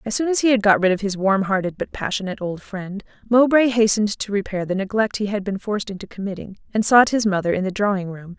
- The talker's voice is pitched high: Yes, high, 205 Hz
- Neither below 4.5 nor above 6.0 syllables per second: No, 6.3 syllables/s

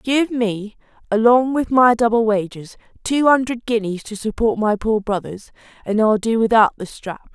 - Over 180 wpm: No, average, 170 wpm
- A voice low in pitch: No, high, 225 Hz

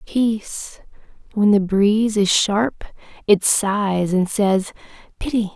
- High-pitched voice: Yes, high, 205 Hz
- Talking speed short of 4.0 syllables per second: Yes, 3.5 syllables/s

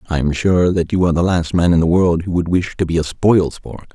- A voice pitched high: No, very low, 85 Hz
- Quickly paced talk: Yes, fast, 305 wpm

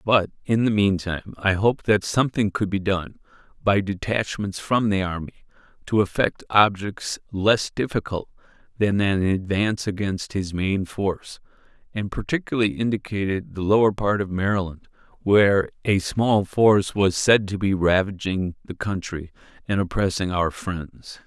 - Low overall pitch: Yes, low, 100 Hz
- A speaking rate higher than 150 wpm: No, average, 145 wpm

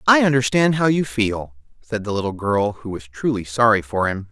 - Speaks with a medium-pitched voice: No, low, 115 Hz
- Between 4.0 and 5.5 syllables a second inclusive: Yes, 5.1 syllables/s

